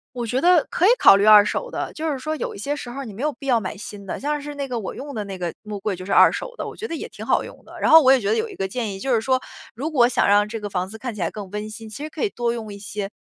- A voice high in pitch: Yes, high, 230 Hz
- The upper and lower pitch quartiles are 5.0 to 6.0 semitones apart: Yes, wide, 5.5 semitones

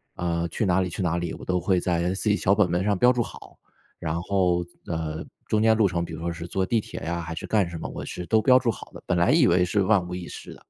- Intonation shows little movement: No, average, 3.3 semitones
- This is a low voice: Yes, very low, 90 Hz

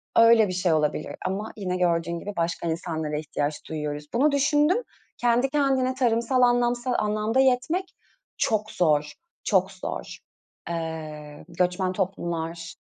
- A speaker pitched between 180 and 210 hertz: Yes, high, 190 Hz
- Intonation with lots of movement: Yes, wide, 6.7 semitones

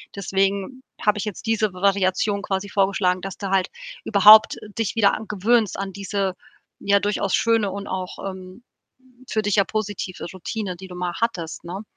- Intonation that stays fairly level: Yes, narrow, 2.0 semitones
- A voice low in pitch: No, high, 200 Hz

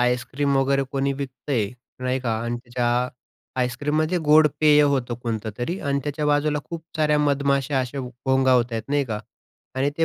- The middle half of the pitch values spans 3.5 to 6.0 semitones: No, average, 2.9 semitones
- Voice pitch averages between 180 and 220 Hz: No, low, 135 Hz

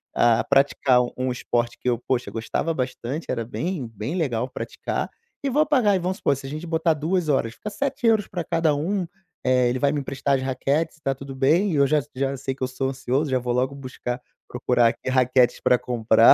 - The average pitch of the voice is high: No, low, 135 Hz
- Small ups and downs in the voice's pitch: No, average, 4.3 semitones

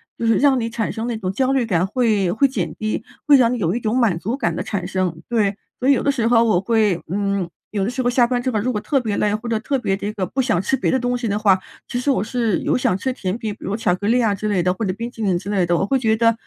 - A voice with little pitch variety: No, average, 3.9 semitones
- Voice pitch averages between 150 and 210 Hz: No, high, 220 Hz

